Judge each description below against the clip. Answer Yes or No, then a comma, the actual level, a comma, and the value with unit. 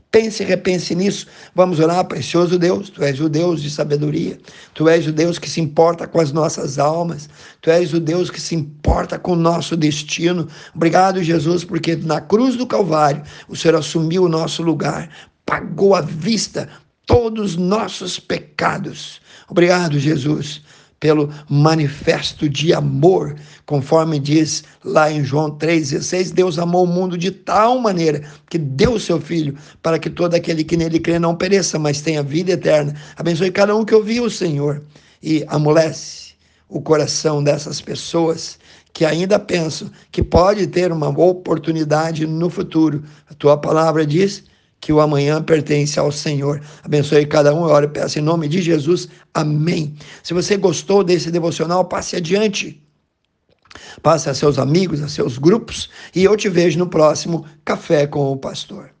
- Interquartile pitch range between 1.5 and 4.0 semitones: Yes, average, 2.9 semitones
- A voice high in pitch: No, medium, 165 Hz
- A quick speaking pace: No, average, 165 wpm